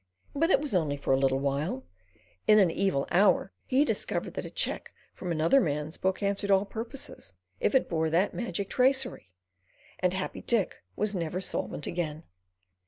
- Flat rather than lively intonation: No, average, 5.3 semitones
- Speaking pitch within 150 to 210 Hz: Yes, medium, 185 Hz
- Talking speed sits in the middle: Yes, average, 170 wpm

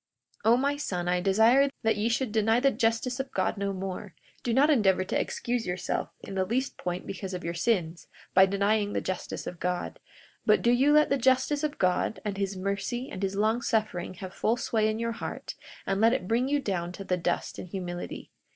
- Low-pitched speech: No, high, 210 Hz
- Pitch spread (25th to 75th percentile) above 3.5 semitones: Yes, average, 4.5 semitones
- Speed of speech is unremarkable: No, fast, 220 wpm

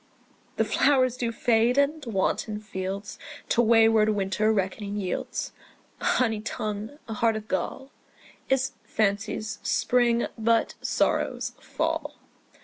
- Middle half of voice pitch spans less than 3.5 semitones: Yes, narrow, 2.5 semitones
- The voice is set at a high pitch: Yes, high, 220 Hz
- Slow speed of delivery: Yes, slow, 120 wpm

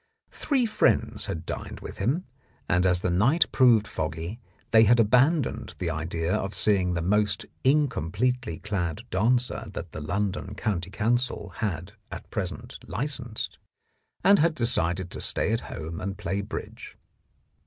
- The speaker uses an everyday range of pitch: No, wide, 5.8 semitones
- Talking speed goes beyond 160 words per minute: No, average, 145 wpm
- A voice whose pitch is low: Yes, low, 105 Hz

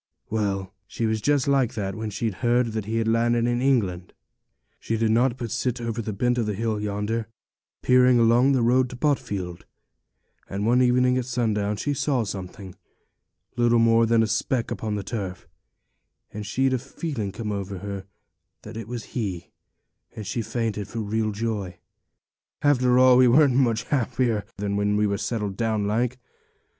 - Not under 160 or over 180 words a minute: Yes, average, 175 wpm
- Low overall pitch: Yes, low, 115 Hz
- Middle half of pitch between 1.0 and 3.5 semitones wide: Yes, average, 3.1 semitones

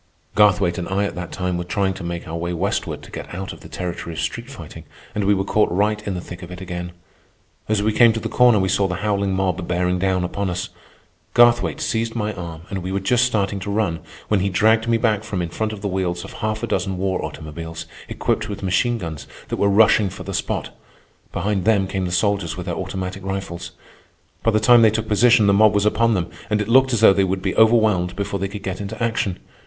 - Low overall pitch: Yes, low, 100 Hz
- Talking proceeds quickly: Yes, fast, 245 wpm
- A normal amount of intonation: Yes, average, 3.1 semitones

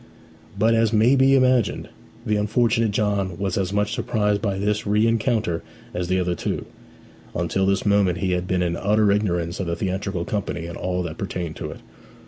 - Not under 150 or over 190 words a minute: Yes, average, 185 wpm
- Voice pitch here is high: No, low, 100 Hz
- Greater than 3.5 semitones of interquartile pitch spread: No, average, 3.0 semitones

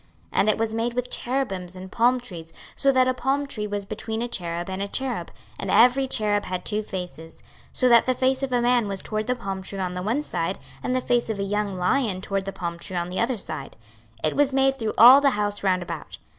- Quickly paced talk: Yes, fast, 255 wpm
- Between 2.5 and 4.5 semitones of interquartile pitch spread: No, average, 5.0 semitones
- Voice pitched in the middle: No, high, 215 Hz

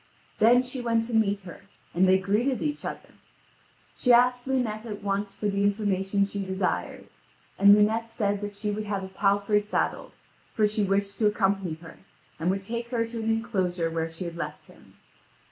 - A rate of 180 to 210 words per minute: Yes, average, 190 wpm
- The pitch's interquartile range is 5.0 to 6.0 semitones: No, average, 2.7 semitones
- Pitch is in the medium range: No, high, 205 Hz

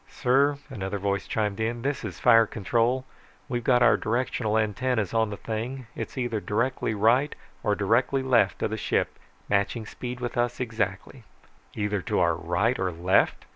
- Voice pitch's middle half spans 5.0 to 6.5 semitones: No, average, 3.3 semitones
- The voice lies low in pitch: Yes, low, 115 Hz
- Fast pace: No, average, 170 wpm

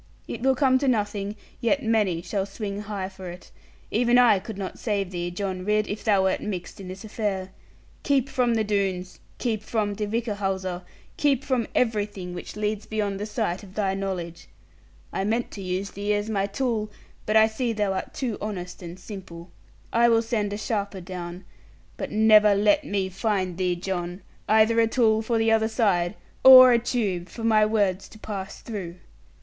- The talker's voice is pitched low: No, high, 205 Hz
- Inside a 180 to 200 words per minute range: Yes, average, 190 wpm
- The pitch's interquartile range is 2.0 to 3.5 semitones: Yes, average, 2.9 semitones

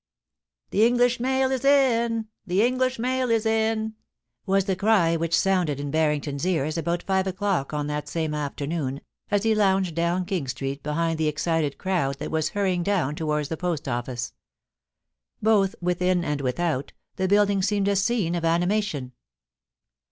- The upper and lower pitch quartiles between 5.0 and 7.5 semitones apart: Yes, wide, 5.5 semitones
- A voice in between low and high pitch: Yes, medium, 180 Hz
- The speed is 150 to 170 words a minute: Yes, average, 165 wpm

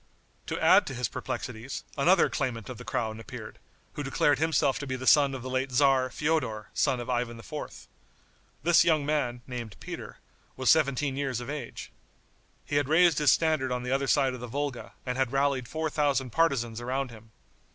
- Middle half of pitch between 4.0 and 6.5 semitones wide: No, average, 2.9 semitones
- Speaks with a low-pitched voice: Yes, low, 130 Hz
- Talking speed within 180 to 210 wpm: Yes, average, 195 wpm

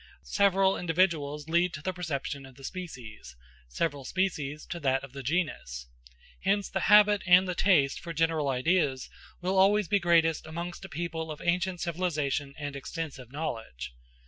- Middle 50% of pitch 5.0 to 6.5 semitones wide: No, average, 4.6 semitones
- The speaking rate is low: No, average, 160 wpm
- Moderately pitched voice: Yes, medium, 165 Hz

